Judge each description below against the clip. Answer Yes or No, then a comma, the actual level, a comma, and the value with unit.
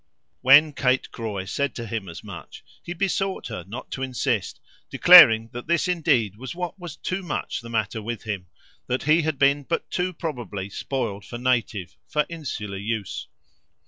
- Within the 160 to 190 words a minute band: Yes, average, 170 wpm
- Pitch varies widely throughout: Yes, wide, 6.0 semitones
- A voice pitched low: Yes, low, 125 Hz